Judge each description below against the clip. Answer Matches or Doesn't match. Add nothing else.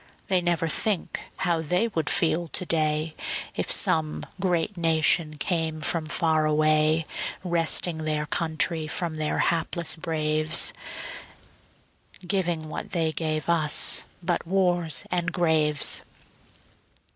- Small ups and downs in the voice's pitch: Matches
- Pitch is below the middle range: Doesn't match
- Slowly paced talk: Matches